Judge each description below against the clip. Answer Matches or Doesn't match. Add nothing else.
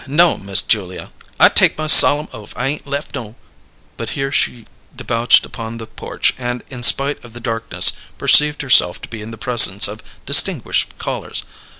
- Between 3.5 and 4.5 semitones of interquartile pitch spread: Matches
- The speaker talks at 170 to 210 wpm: Matches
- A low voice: Matches